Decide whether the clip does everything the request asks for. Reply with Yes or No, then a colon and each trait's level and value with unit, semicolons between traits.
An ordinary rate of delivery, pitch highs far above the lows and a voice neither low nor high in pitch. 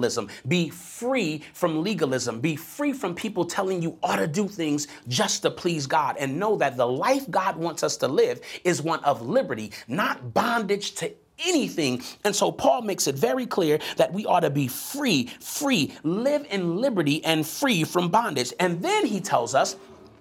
Yes: average, 185 wpm; wide, 7.4 semitones; medium, 175 Hz